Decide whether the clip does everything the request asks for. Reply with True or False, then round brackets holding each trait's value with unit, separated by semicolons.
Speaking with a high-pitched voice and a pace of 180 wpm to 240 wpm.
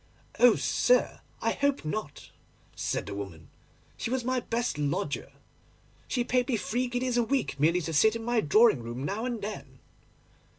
False (225 Hz; 170 wpm)